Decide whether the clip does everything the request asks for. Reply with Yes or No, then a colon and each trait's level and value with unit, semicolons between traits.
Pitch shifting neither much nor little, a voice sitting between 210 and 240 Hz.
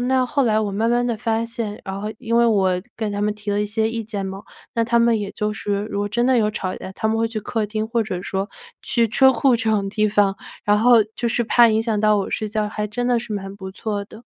No: narrow, 2.1 semitones; high, 215 Hz